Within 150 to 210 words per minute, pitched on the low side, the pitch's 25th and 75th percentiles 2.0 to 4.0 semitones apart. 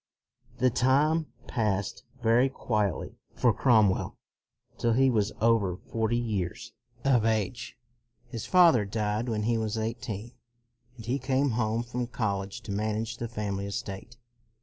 No: average, 140 wpm; low, 115 Hz; average, 2.7 semitones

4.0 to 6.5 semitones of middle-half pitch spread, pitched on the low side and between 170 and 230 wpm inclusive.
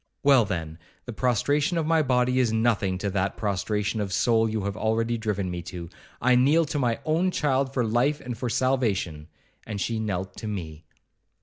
Yes: average, 4.5 semitones; low, 115 Hz; average, 190 wpm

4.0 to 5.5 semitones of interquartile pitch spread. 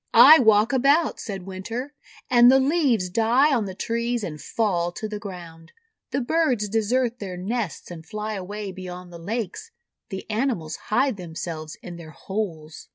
Yes: average, 5.1 semitones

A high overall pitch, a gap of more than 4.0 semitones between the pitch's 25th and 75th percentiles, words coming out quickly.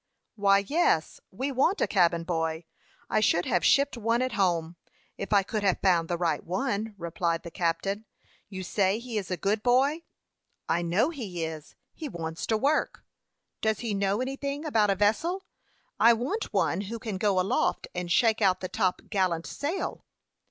No: high, 200 Hz; average, 5.1 semitones; average, 180 wpm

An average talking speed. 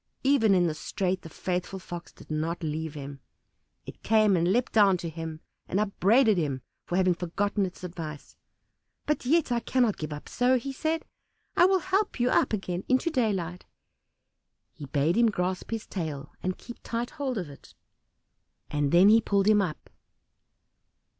Yes: average, 175 wpm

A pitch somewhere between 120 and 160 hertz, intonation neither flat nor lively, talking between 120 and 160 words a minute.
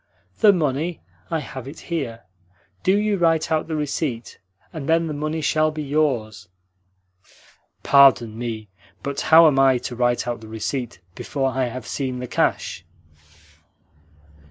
Yes: medium, 140 Hz; average, 4.5 semitones; average, 150 wpm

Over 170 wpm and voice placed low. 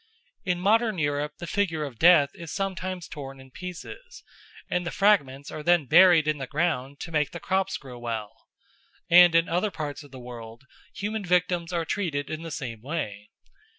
No: average, 185 wpm; medium, 165 Hz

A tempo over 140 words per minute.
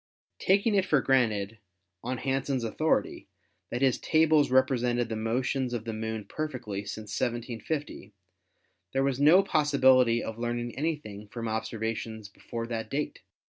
No: slow, 135 wpm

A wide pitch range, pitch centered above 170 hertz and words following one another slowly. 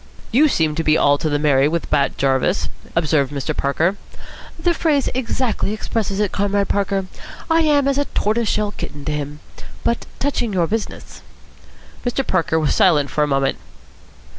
No: wide, 7.6 semitones; medium, 185 Hz; average, 165 wpm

